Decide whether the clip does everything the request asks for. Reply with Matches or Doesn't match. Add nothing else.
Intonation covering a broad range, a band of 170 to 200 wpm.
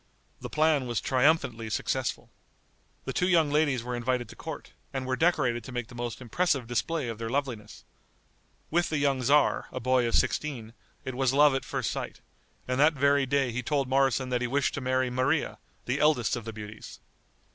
Doesn't match